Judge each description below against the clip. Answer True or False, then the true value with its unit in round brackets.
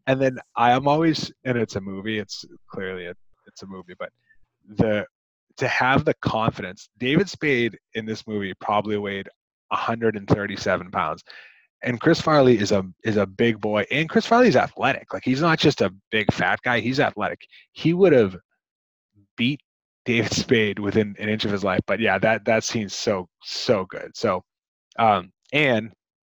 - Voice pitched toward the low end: True (110 Hz)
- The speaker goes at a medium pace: True (170 wpm)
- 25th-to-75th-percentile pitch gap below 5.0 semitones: True (4.6 semitones)